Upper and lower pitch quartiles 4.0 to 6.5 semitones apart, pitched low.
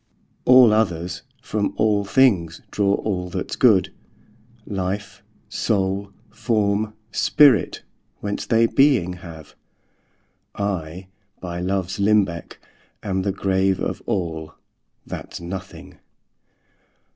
No: average, 2.8 semitones; very low, 95 Hz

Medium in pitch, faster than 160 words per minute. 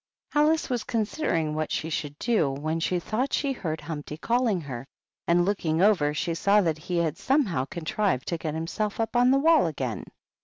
Yes: medium, 170 Hz; average, 195 wpm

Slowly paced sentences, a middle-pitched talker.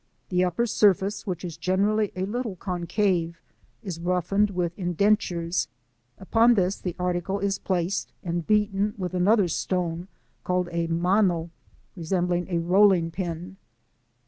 Yes: slow, 130 wpm; medium, 180 Hz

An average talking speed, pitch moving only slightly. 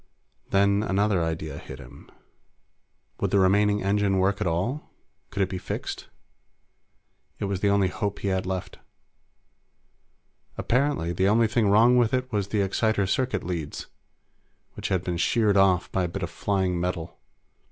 Yes: average, 160 wpm; narrow, 2.2 semitones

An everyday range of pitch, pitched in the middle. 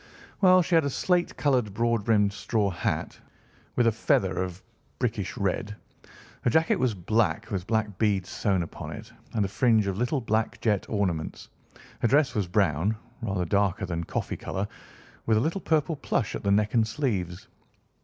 No: average, 3.8 semitones; low, 105 Hz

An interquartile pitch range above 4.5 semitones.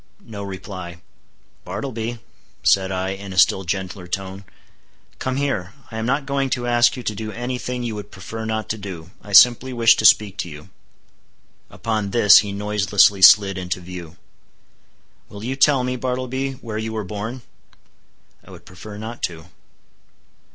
No: average, 4.0 semitones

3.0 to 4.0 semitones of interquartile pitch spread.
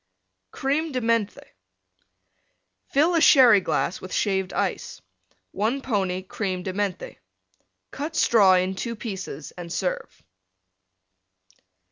No: average, 5.3 semitones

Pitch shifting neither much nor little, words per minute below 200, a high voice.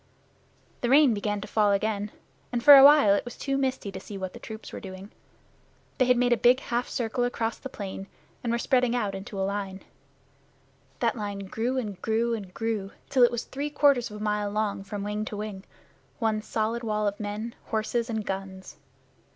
No: average, 3.1 semitones; fast, 205 wpm; high, 220 Hz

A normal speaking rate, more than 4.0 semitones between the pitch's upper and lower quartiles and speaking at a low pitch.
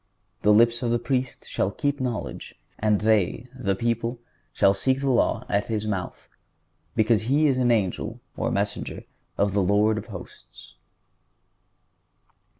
No: average, 150 wpm; average, 3.4 semitones; low, 115 Hz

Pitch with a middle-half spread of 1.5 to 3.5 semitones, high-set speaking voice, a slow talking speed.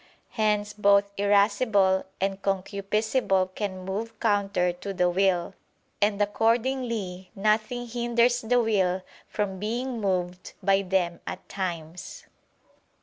Yes: average, 2.8 semitones; high, 200 Hz; slow, 110 wpm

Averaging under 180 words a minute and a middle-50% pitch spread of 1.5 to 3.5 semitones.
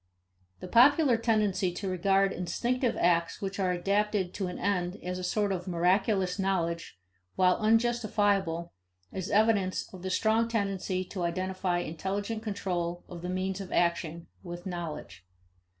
Yes: average, 145 wpm; average, 2.7 semitones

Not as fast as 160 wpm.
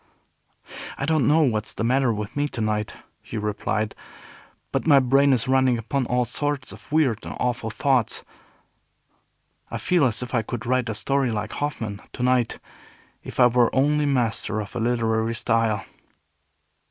No: average, 165 wpm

